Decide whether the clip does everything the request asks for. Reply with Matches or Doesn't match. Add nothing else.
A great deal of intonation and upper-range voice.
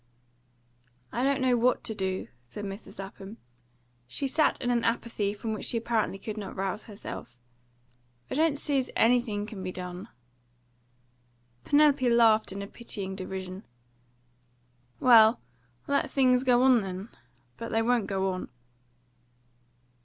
Doesn't match